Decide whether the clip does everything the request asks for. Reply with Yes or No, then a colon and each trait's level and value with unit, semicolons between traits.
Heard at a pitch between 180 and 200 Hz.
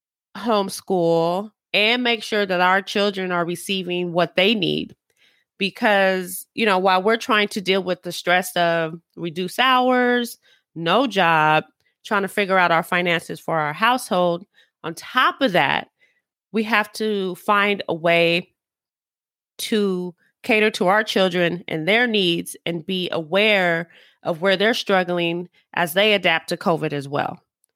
Yes: high, 190 Hz